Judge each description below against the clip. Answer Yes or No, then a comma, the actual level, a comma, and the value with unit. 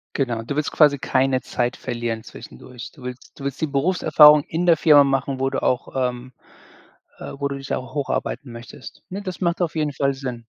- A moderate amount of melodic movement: Yes, average, 3.0 semitones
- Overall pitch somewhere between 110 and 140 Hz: Yes, low, 135 Hz